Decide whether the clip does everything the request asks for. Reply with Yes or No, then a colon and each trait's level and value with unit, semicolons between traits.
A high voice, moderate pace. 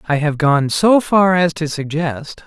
No: medium, 160 Hz; average, 195 wpm